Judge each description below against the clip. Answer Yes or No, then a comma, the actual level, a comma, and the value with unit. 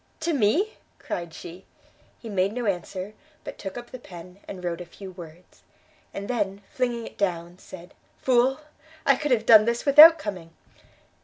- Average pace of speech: Yes, average, 170 wpm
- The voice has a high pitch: Yes, high, 205 Hz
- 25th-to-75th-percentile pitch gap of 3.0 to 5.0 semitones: No, wide, 5.4 semitones